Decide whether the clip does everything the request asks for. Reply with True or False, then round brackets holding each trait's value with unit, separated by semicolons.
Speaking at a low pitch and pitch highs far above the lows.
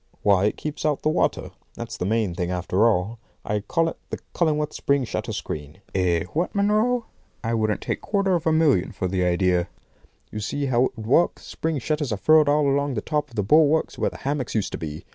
True (130 Hz; 8.0 semitones)